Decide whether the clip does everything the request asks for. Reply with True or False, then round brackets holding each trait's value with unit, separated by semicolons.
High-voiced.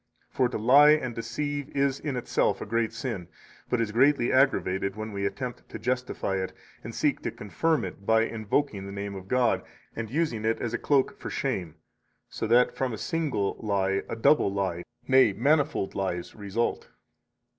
False (115 Hz)